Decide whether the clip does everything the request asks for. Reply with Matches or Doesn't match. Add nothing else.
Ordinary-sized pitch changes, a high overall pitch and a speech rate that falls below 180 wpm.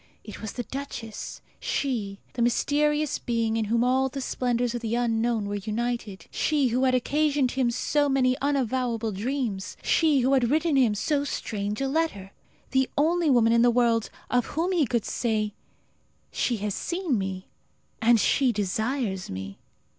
Matches